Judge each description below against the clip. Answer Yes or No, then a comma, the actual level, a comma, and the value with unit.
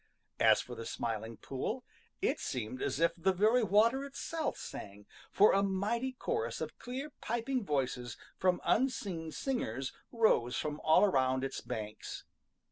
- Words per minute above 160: No, average, 145 wpm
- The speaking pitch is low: No, medium, 185 Hz